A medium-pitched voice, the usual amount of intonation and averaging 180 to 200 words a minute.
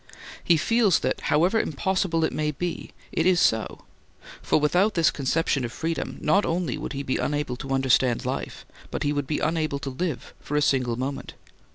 Yes: medium, 150 Hz; average, 4.1 semitones; average, 190 wpm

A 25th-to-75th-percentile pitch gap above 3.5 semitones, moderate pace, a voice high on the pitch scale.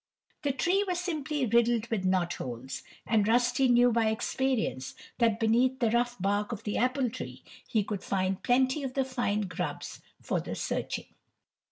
Yes: average, 4.0 semitones; average, 165 wpm; high, 235 Hz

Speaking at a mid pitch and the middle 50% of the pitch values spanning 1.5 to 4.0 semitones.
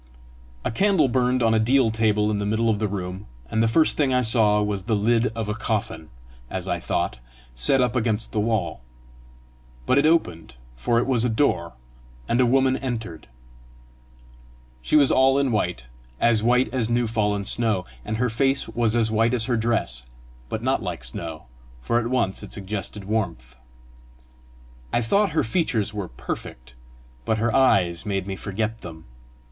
No: low, 110 Hz; average, 3.7 semitones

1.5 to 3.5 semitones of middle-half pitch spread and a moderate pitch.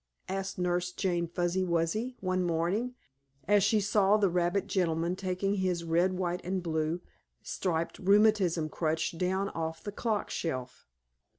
Yes: narrow, 2.6 semitones; medium, 180 Hz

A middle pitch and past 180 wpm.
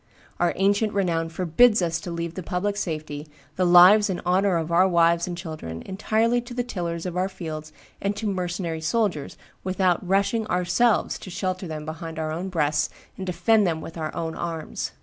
Yes: medium, 180 Hz; average, 190 wpm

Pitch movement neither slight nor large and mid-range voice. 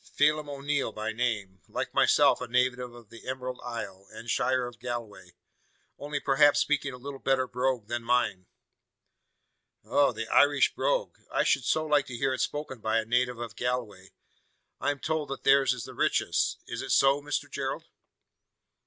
No: average, 3.4 semitones; low, 125 Hz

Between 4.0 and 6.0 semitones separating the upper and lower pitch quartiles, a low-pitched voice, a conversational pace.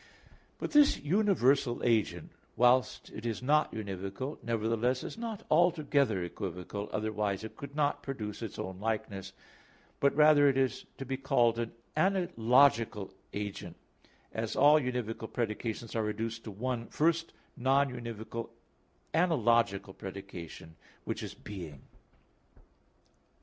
No: average, 5.0 semitones; low, 115 Hz; slow, 125 wpm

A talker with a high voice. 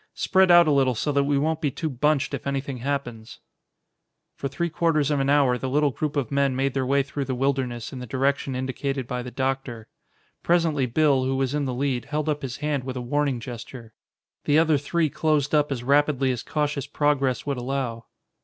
No: medium, 140 Hz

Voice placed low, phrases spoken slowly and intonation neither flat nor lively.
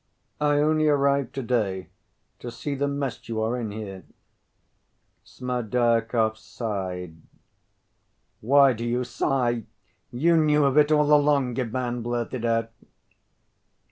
Yes: low, 125 Hz; slow, 115 wpm; average, 3.7 semitones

